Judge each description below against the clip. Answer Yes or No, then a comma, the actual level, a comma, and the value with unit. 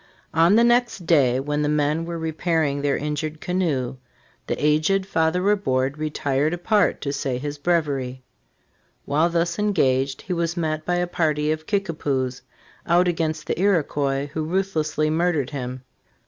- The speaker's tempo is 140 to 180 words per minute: Yes, average, 155 wpm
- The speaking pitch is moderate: Yes, medium, 155 Hz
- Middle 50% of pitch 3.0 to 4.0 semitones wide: Yes, average, 3.4 semitones